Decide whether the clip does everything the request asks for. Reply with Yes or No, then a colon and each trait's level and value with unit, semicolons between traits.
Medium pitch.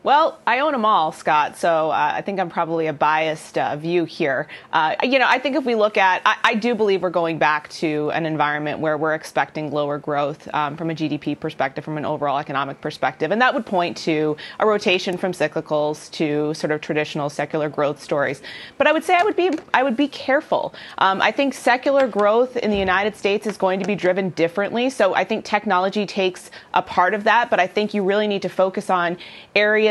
Yes: medium, 180 Hz